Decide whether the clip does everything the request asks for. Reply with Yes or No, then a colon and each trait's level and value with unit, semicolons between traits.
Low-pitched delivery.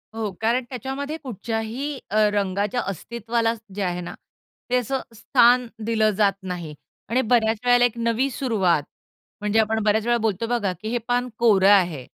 No: high, 225 Hz